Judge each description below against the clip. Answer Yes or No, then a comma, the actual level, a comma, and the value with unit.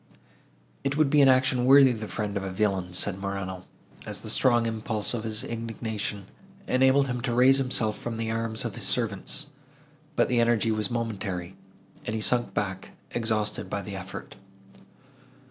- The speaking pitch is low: Yes, low, 110 Hz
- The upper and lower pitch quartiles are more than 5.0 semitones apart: No, average, 3.3 semitones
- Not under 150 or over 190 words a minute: Yes, average, 170 wpm